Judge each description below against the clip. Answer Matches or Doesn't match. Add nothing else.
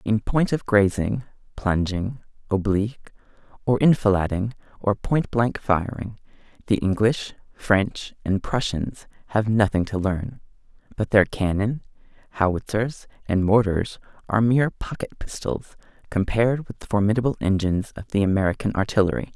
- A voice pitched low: Matches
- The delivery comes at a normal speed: Doesn't match